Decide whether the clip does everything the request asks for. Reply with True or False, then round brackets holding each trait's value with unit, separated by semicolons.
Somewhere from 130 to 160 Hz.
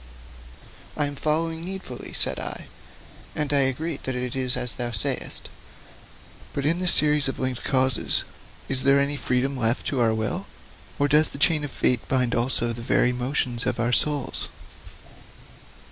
True (135 Hz)